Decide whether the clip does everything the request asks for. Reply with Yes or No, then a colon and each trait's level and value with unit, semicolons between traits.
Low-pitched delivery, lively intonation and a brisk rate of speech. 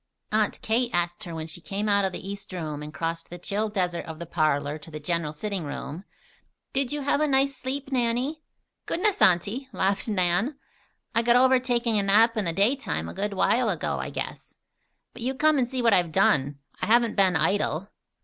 No: high, 200 Hz; wide, 6.2 semitones; fast, 210 wpm